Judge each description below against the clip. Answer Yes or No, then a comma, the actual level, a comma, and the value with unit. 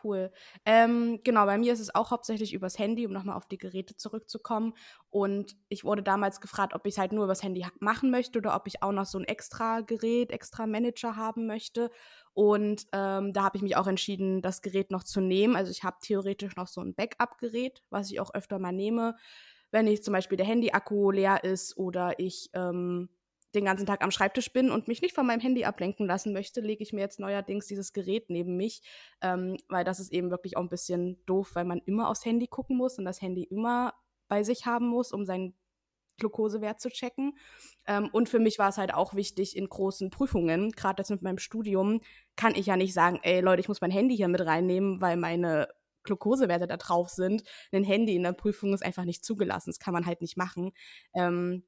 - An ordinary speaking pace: No, fast, 220 wpm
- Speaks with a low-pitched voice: No, high, 200 Hz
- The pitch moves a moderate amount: Yes, average, 3.2 semitones